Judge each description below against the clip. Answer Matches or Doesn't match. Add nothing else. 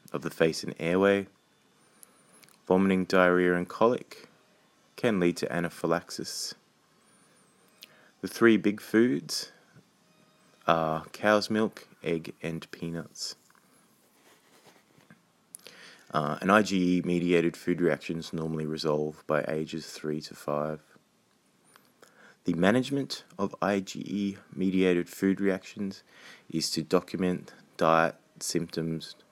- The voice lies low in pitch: Matches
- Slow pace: Matches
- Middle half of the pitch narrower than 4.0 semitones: Matches